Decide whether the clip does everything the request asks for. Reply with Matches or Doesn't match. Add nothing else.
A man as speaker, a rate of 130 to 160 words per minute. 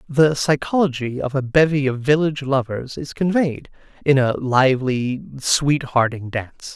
Matches